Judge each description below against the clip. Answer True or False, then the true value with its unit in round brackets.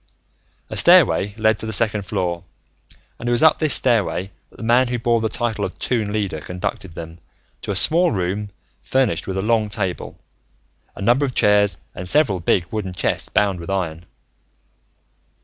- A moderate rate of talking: True (180 wpm)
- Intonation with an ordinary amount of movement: True (3.9 semitones)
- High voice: False (105 Hz)